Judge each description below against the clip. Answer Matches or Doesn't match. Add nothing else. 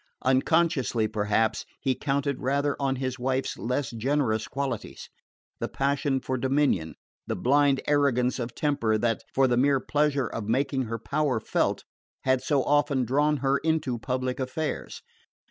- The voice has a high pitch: Doesn't match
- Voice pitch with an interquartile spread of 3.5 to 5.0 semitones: Doesn't match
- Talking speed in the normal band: Matches